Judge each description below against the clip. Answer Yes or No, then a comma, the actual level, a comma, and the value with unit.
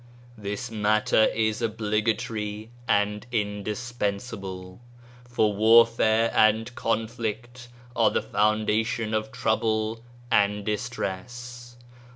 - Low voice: Yes, low, 110 Hz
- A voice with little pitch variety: Yes, narrow, 1.9 semitones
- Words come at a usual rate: No, slow, 85 wpm